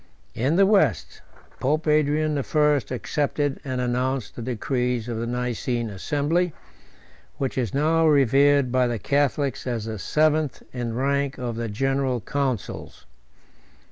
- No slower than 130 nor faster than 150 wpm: Yes, average, 140 wpm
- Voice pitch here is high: No, low, 135 Hz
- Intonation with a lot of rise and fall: No, average, 3.2 semitones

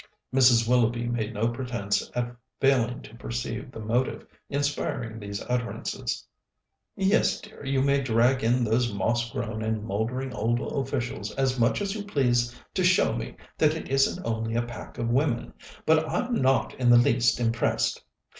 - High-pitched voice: No, low, 120 Hz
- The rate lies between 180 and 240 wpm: No, average, 165 wpm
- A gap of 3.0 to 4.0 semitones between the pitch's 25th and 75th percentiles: No, narrow, 2.6 semitones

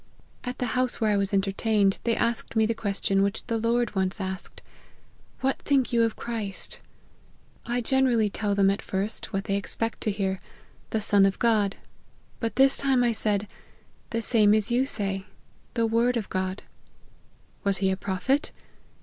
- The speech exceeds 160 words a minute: Yes, average, 190 wpm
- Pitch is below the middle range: No, high, 215 Hz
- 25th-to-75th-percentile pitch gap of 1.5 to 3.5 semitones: Yes, average, 3.1 semitones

